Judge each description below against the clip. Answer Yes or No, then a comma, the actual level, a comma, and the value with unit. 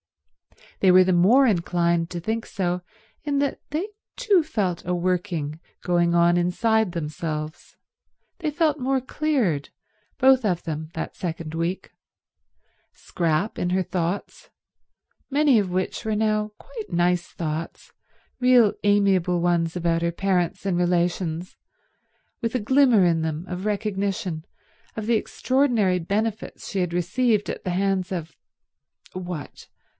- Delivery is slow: Yes, slow, 130 wpm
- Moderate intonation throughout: Yes, average, 4.3 semitones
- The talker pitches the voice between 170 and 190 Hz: Yes, medium, 185 Hz